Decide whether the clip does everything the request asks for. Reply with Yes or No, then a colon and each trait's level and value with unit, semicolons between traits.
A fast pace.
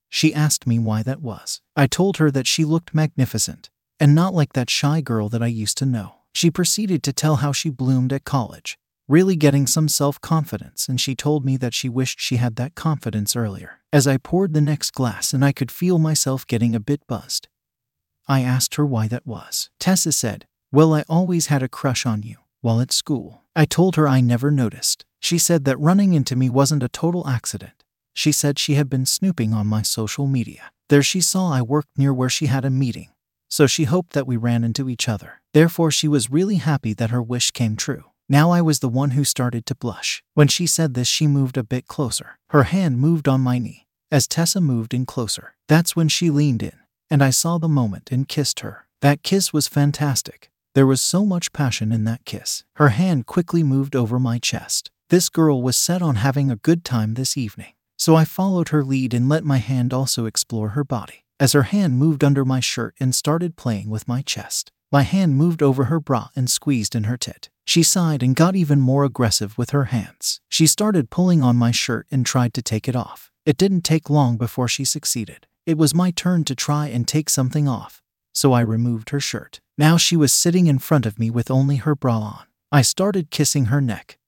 Yes: fast, 220 wpm